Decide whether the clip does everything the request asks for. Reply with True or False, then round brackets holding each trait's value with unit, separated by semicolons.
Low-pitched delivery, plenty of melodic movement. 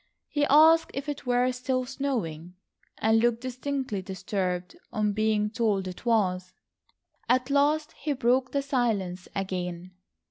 False (235 Hz; 6.0 semitones)